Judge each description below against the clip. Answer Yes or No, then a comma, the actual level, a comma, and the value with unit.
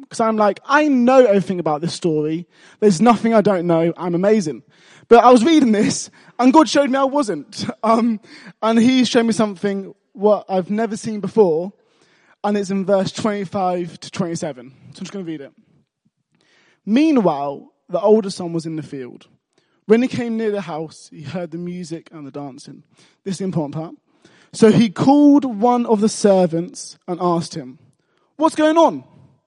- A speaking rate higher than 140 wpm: Yes, average, 185 wpm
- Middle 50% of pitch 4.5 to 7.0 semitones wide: Yes, wide, 5.5 semitones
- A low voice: No, high, 200 Hz